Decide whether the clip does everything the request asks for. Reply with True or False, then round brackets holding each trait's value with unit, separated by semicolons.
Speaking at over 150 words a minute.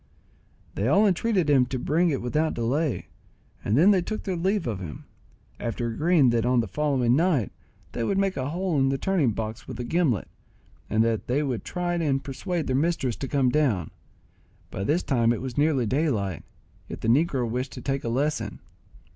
True (195 wpm)